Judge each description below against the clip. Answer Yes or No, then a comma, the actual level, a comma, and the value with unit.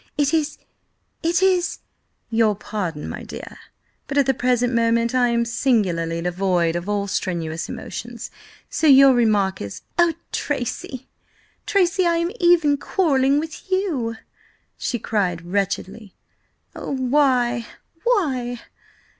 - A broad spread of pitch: Yes, wide, 6.6 semitones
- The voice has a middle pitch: No, high, 245 Hz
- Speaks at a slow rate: Yes, slow, 120 wpm